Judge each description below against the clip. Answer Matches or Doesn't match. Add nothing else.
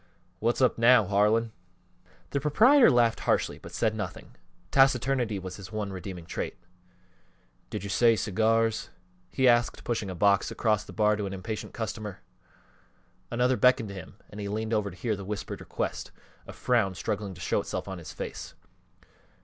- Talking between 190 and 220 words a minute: Doesn't match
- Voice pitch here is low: Matches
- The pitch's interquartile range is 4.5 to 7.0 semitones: Doesn't match